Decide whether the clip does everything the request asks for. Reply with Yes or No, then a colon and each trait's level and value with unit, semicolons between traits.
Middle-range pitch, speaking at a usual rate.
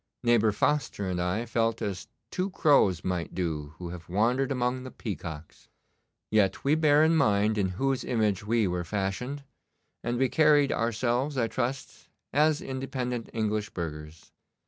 No: low, 115 Hz; average, 150 wpm